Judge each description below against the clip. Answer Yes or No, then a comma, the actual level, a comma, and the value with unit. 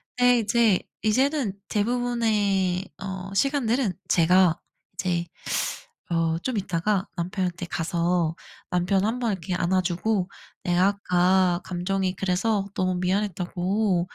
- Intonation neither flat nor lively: Yes, average, 3.1 semitones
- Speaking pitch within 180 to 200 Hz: Yes, high, 190 Hz